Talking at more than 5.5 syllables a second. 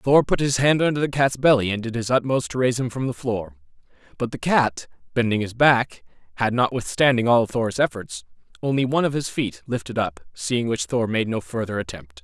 No: 5.4 syllables/s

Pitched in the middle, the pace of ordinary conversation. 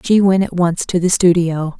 No: medium, 175 Hz; fast, 235 wpm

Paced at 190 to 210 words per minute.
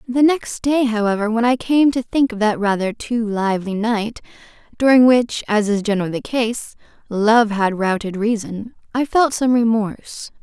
No: average, 175 wpm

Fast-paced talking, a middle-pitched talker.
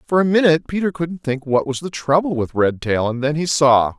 Yes: fast, 240 wpm; medium, 150 Hz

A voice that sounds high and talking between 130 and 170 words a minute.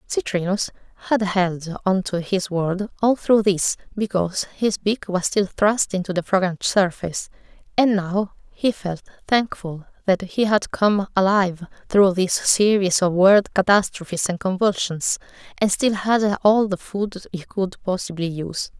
Yes: high, 195 Hz; average, 155 wpm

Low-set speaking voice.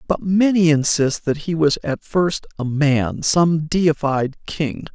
No: medium, 155 Hz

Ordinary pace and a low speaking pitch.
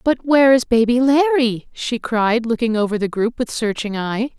No: average, 190 wpm; high, 235 Hz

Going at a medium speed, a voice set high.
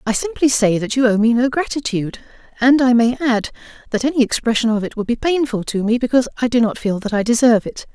No: fast, 240 wpm; high, 240 Hz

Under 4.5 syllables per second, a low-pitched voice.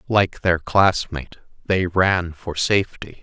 Yes: 4.0 syllables/s; very low, 90 Hz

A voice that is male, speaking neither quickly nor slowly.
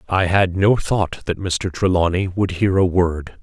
Yes: male; average, 195 wpm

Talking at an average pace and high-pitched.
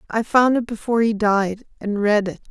Yes: average, 190 wpm; high, 215 Hz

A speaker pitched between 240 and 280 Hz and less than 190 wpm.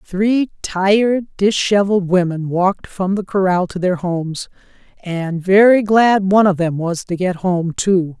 No: high, 190 Hz; average, 160 wpm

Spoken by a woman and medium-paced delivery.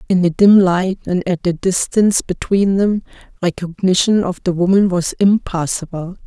Yes: female; average, 155 wpm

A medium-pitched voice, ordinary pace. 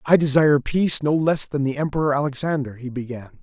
Yes: medium, 145 Hz; average, 195 wpm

